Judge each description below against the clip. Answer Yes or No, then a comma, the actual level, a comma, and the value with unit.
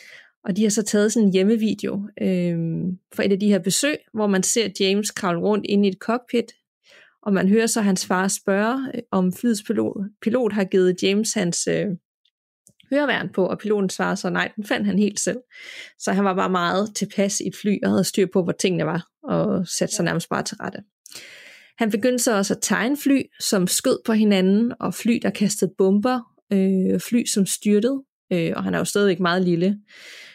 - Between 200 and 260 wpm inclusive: Yes, average, 205 wpm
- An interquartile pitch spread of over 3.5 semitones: No, average, 3.1 semitones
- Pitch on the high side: Yes, high, 200 Hz